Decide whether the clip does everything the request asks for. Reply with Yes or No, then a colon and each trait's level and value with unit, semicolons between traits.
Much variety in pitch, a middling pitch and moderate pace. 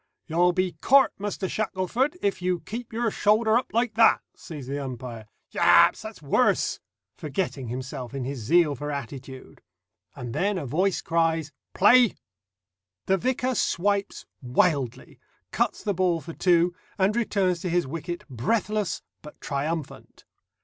Yes: wide, 6.5 semitones; medium, 175 Hz; average, 150 wpm